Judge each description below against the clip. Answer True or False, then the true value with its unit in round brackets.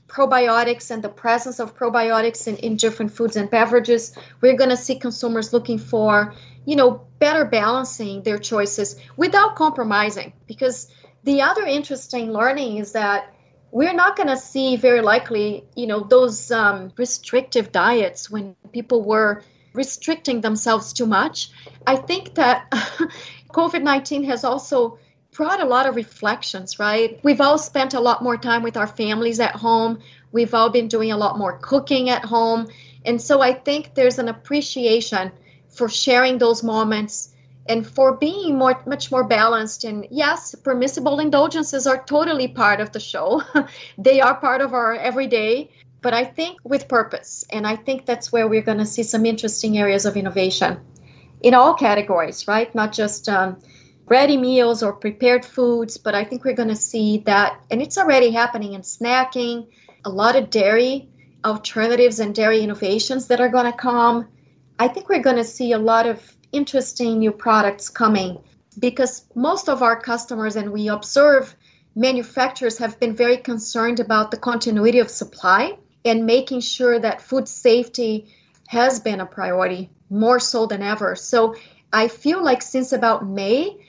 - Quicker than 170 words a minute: False (165 wpm)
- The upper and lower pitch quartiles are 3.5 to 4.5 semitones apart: False (3.1 semitones)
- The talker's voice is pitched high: True (235 Hz)